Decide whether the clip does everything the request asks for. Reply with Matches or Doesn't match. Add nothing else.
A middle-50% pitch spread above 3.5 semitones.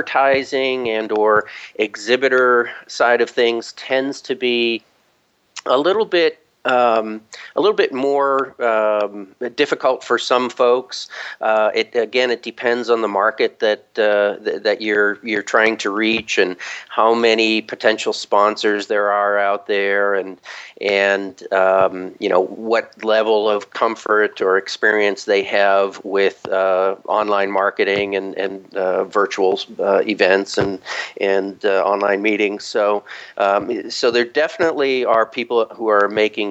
Doesn't match